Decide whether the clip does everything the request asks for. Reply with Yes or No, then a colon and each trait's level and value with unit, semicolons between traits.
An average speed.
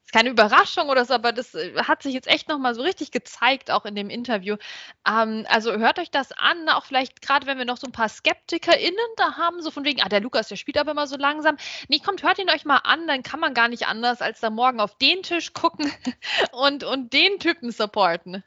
No: fast, 245 wpm